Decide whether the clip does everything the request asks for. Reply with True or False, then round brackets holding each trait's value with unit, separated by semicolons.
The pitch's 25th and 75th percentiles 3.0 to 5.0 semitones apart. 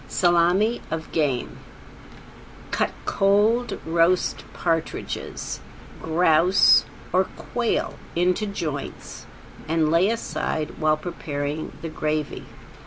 True (3.4 semitones)